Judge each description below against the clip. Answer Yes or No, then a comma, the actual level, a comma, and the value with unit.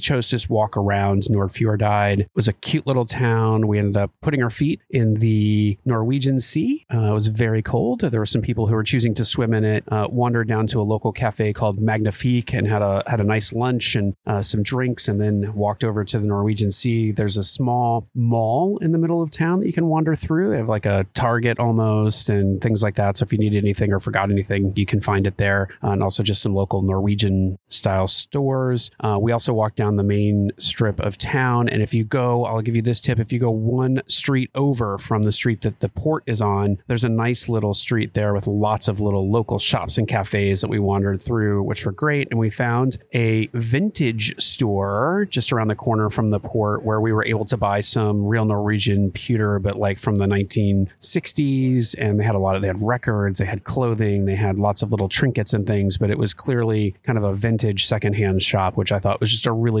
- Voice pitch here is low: Yes, low, 110 Hz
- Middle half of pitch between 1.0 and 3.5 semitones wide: Yes, average, 2.8 semitones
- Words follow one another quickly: Yes, fast, 230 wpm